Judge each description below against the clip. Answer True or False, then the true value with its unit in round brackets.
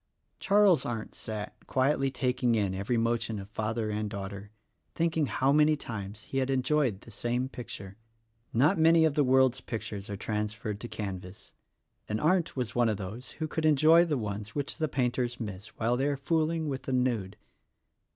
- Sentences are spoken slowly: False (185 wpm)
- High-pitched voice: False (120 Hz)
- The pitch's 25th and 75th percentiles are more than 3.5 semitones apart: True (5.2 semitones)